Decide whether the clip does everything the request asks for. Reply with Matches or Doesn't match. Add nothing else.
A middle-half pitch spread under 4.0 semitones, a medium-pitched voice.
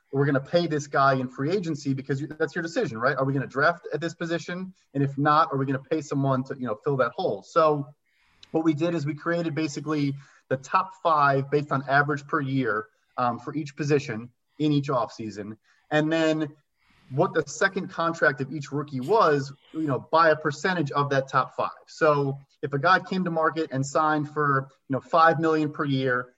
Matches